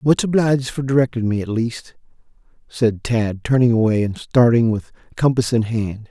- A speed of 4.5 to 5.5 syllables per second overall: Yes, 5.0 syllables/s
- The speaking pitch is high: No, low, 120 Hz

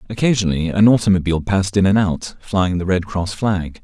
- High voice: No, very low, 95 Hz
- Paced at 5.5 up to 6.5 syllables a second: Yes, 5.8 syllables/s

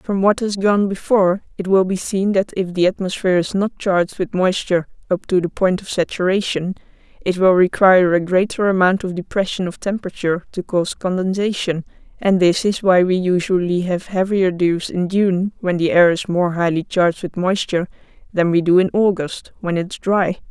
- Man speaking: No, female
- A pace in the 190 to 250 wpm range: Yes, average, 195 wpm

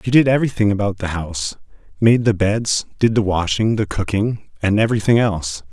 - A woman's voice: No, male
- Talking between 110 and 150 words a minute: No, average, 170 wpm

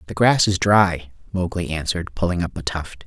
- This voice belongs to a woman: No, male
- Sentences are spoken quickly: No, average, 195 wpm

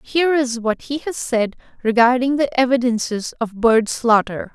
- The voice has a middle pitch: No, high, 245 Hz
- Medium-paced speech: Yes, average, 160 wpm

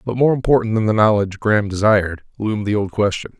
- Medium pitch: No, low, 105 Hz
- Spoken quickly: Yes, fast, 210 wpm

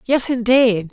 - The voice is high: Yes, high, 240 Hz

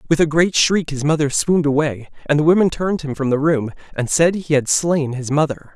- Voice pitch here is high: No, medium, 150 Hz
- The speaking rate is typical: No, fast, 240 wpm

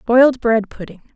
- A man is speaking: No, female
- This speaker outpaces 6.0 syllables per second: No, 5.4 syllables/s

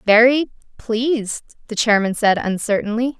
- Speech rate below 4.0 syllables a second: No, 4.9 syllables/s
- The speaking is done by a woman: Yes, female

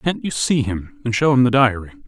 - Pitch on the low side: Yes, low, 130 Hz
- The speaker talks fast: Yes, fast, 260 wpm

